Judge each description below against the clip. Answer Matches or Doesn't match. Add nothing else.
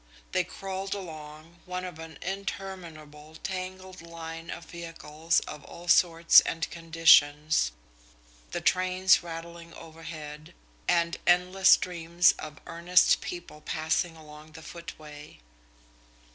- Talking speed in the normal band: Doesn't match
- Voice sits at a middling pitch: Matches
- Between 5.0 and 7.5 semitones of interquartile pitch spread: Doesn't match